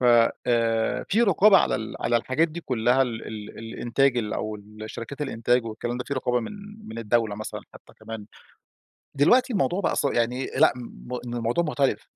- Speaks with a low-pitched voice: Yes, low, 120 Hz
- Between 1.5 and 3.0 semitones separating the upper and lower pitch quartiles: No, average, 3.8 semitones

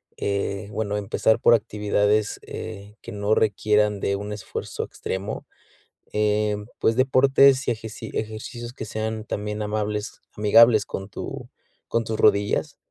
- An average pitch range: No, narrow, 1.3 semitones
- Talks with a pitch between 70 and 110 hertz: Yes, low, 105 Hz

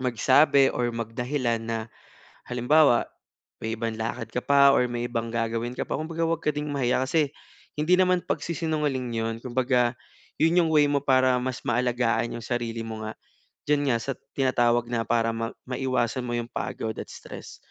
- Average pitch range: Yes, average, 3.3 semitones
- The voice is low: Yes, low, 125 Hz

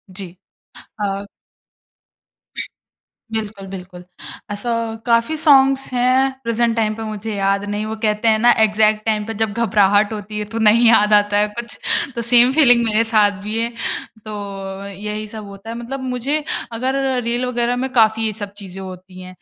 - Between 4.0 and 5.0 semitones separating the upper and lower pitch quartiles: No, narrow, 2.5 semitones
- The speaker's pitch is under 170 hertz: No, high, 215 Hz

